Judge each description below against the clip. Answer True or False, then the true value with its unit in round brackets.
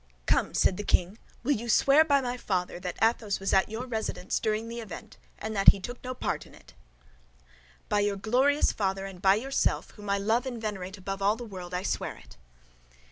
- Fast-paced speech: True (210 wpm)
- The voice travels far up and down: False (3.6 semitones)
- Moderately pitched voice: False (210 Hz)